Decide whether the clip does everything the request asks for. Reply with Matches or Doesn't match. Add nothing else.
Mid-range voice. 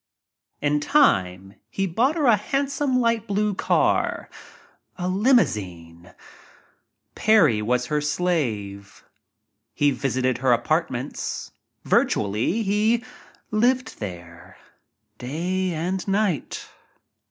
Matches